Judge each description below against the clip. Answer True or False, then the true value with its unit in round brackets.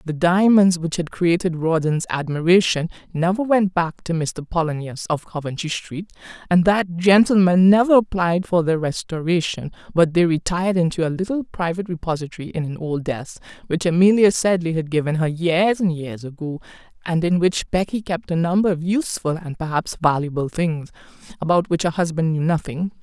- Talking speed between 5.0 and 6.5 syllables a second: True (5.2 syllables/s)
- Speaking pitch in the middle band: True (170 Hz)